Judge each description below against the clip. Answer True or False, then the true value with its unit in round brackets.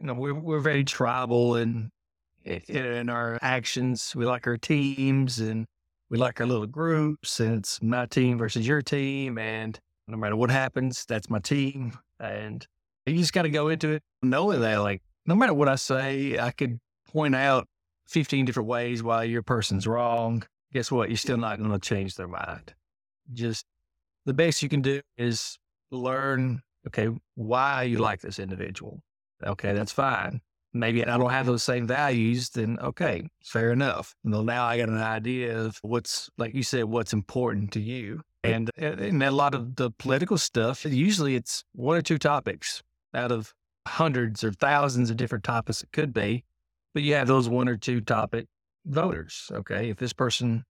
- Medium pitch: False (120 Hz)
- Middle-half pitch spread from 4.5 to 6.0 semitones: False (3.3 semitones)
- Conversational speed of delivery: True (180 wpm)